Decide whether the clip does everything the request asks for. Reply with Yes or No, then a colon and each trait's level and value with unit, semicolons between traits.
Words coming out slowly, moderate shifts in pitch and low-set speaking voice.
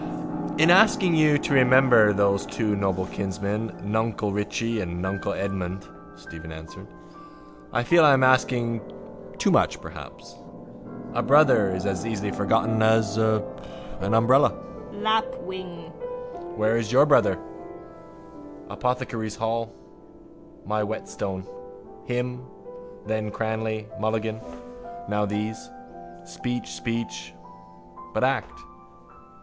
Yes: slow, 105 wpm; average, 3.8 semitones; low, 110 Hz